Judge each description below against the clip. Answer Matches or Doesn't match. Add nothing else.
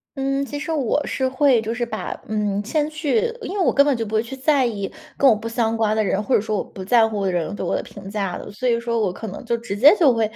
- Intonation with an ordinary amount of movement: Matches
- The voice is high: Matches